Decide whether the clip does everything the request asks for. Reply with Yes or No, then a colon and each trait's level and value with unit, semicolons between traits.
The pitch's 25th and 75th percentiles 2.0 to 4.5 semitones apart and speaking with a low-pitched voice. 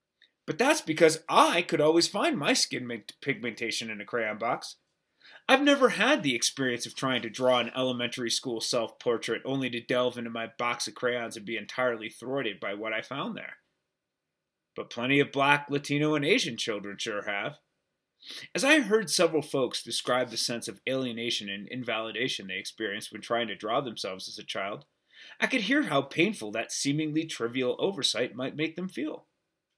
No: average, 5.1 semitones; low, 125 Hz